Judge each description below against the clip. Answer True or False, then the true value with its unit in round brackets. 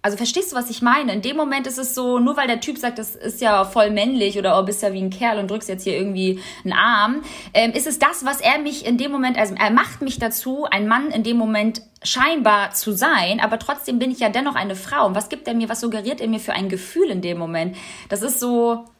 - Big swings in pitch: False (4.1 semitones)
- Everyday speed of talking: False (265 wpm)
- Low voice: False (230 Hz)